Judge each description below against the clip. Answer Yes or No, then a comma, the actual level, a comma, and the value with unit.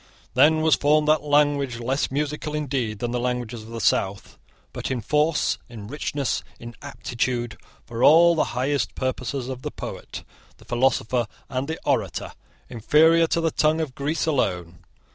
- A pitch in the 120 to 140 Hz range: Yes, low, 135 Hz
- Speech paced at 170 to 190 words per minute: No, average, 160 wpm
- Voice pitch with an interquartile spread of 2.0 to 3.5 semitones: No, average, 4.0 semitones